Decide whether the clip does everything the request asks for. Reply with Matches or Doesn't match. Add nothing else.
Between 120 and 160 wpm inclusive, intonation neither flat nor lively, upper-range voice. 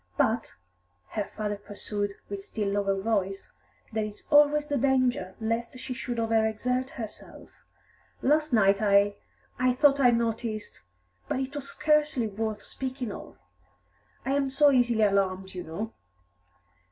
Matches